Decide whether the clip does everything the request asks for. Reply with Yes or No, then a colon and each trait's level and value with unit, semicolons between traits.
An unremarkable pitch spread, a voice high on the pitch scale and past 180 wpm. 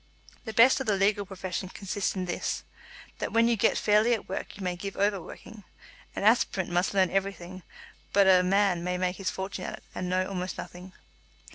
No: narrow, 1.9 semitones; high, 195 Hz; fast, 205 wpm